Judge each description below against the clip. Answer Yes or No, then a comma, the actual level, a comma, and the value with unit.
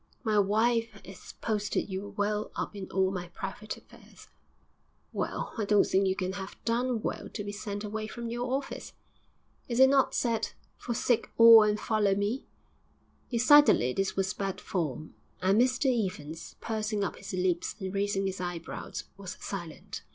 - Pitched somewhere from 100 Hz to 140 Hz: No, high, 205 Hz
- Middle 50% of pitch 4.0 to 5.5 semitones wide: No, average, 3.2 semitones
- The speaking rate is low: No, average, 165 wpm